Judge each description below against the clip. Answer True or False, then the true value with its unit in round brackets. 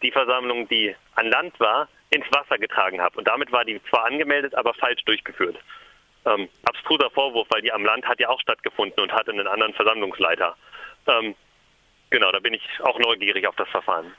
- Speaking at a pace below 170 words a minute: False (190 wpm)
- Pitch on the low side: True (125 Hz)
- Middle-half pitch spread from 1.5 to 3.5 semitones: True (3.0 semitones)